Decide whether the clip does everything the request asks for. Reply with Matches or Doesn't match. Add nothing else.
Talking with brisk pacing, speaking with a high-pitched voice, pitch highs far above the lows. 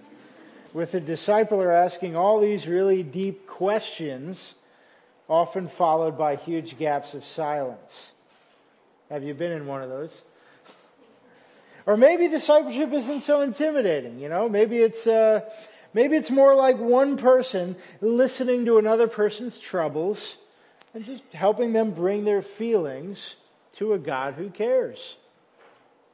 Doesn't match